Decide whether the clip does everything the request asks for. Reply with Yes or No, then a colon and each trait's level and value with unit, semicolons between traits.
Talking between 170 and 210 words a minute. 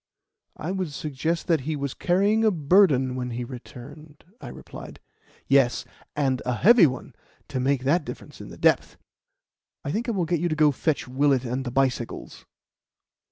Yes: average, 180 wpm